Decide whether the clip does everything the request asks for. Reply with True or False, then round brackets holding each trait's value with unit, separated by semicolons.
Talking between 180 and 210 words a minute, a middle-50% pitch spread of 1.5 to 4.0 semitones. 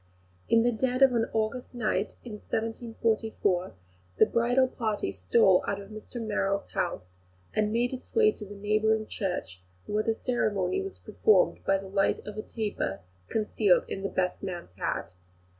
False (165 wpm; 3.1 semitones)